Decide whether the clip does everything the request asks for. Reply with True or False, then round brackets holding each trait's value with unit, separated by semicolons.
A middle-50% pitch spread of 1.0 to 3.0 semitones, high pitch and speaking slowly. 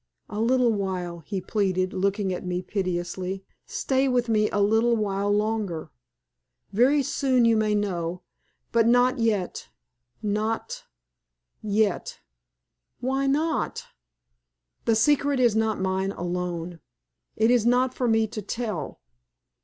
False (4.2 semitones; 215 Hz; 130 wpm)